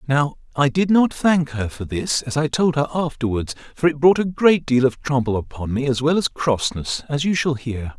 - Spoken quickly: Yes, fast, 235 wpm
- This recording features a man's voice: Yes, male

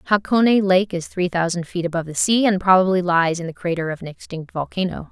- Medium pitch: Yes, medium, 180 Hz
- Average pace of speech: No, fast, 225 wpm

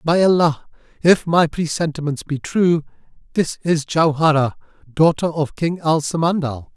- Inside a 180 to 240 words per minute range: No, slow, 135 wpm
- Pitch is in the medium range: Yes, medium, 160 Hz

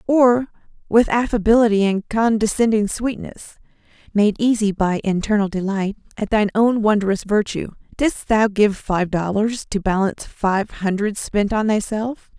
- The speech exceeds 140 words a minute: No, slow, 135 wpm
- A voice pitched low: No, high, 210 Hz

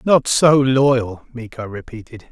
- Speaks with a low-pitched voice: Yes, low, 125 Hz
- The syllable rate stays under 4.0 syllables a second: Yes, 3.8 syllables/s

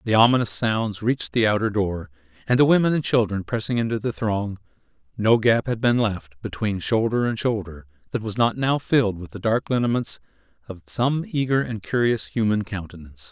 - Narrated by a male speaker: Yes, male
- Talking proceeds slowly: No, average, 185 wpm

